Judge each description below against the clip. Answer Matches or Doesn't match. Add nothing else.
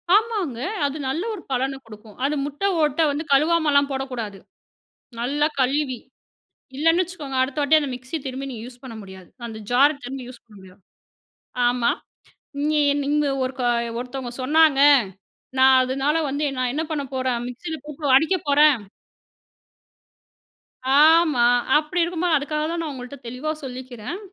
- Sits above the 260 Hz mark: Matches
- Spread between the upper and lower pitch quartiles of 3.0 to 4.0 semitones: Matches